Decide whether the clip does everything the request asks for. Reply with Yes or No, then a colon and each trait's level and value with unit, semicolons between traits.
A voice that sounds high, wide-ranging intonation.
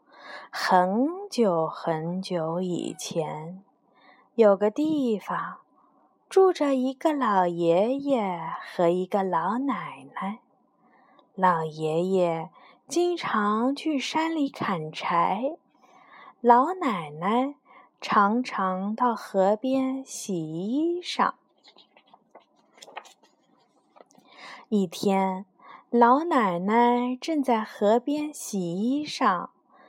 Yes: high, 235 Hz; wide, 6.6 semitones